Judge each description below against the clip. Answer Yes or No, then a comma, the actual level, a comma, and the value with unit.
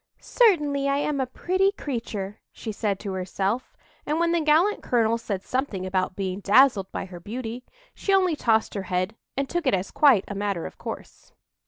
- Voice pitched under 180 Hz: No, high, 230 Hz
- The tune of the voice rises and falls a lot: Yes, wide, 7.0 semitones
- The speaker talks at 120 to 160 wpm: No, average, 190 wpm